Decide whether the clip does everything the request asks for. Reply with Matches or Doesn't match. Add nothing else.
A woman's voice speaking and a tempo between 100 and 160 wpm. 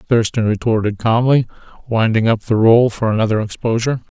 Doesn't match